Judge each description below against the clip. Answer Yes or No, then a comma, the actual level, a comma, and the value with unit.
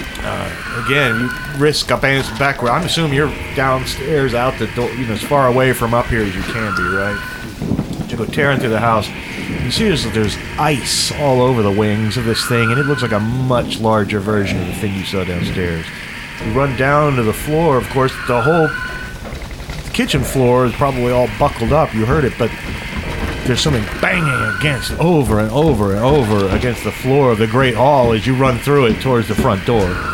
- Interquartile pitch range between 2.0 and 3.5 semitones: No, average, 4.2 semitones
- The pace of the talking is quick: Yes, fast, 210 wpm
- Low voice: Yes, low, 120 Hz